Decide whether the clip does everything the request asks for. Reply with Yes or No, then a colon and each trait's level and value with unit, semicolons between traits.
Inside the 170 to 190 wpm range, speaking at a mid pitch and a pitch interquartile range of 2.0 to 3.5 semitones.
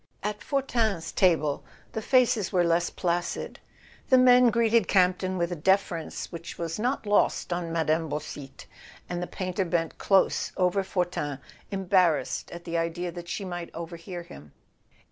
No: average, 155 wpm; medium, 175 Hz; average, 2.9 semitones